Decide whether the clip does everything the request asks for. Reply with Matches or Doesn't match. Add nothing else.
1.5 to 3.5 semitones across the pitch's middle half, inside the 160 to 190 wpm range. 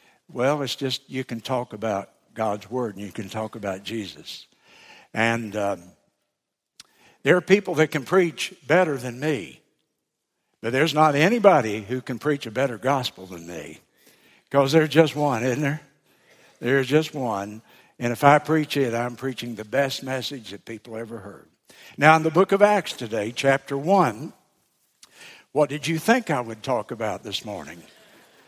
Doesn't match